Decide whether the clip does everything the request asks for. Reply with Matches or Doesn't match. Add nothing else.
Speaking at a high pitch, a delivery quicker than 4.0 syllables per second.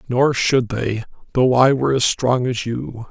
Doesn't match